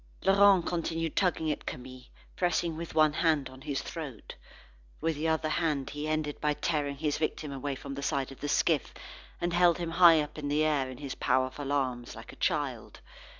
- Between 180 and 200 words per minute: Yes, average, 195 wpm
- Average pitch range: Yes, average, 3.0 semitones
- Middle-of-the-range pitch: Yes, medium, 150 Hz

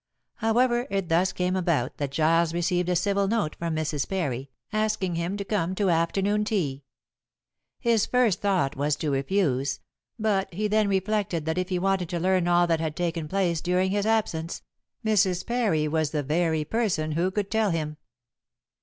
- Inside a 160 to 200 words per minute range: Yes, average, 175 wpm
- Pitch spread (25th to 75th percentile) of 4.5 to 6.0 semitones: No, average, 4.0 semitones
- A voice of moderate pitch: Yes, medium, 180 Hz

